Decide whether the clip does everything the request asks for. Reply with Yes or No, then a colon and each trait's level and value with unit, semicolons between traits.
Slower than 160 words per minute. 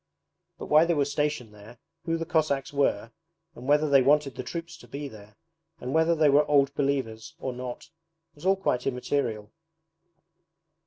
No: average, 170 wpm